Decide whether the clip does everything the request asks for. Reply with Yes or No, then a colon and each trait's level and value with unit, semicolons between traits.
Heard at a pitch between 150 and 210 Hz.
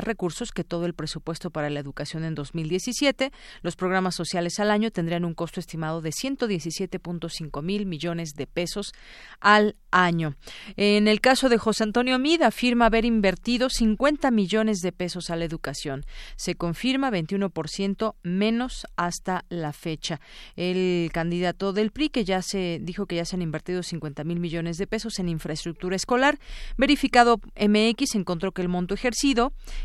Yes: medium, 185 Hz